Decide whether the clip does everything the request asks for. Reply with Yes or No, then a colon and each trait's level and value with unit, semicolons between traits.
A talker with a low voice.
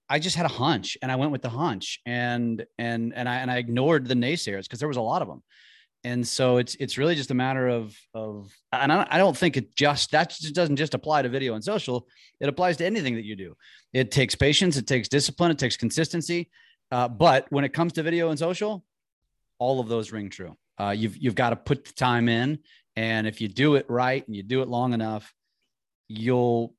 Yes: low, 130 Hz